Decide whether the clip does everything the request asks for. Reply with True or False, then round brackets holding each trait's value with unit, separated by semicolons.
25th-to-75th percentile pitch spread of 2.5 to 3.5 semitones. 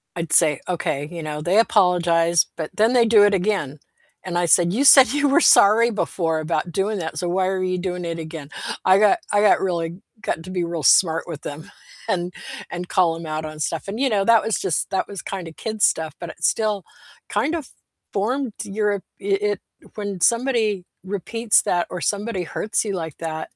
False (4.1 semitones)